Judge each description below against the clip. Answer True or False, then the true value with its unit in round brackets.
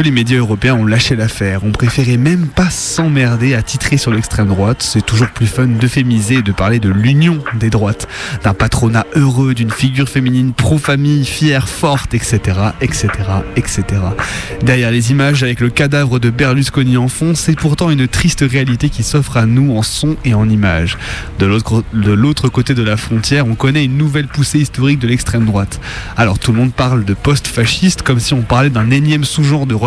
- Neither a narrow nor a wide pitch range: True (3.8 semitones)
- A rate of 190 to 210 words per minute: True (195 wpm)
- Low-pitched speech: True (125 Hz)